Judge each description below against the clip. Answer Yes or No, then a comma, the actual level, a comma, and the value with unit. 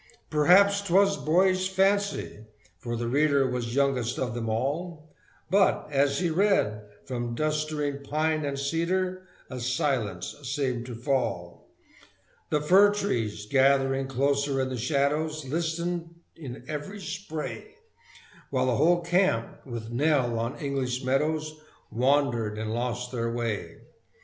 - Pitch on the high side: No, medium, 140 Hz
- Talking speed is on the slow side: Yes, slow, 130 wpm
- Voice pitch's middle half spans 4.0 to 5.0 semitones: Yes, average, 4.7 semitones